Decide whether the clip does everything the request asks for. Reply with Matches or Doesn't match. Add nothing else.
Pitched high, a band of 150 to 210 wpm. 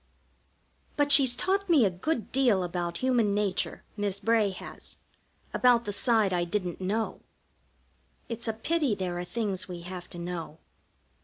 Matches